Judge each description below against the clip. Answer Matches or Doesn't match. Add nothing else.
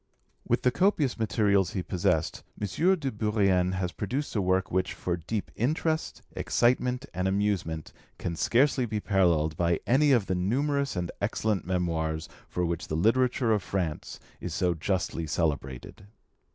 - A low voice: Matches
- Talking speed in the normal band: Matches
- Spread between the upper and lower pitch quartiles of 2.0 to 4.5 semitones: Doesn't match